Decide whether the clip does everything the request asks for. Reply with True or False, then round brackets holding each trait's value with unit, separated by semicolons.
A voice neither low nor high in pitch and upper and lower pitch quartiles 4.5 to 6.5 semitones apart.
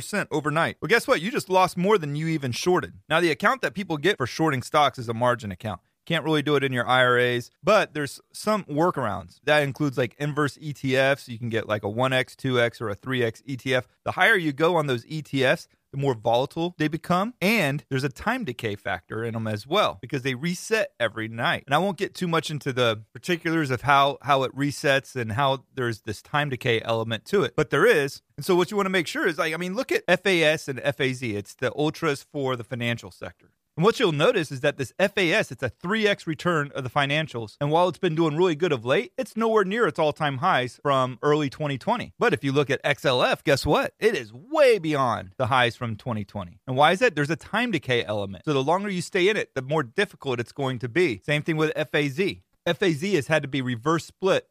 True (145 Hz; 5.4 semitones)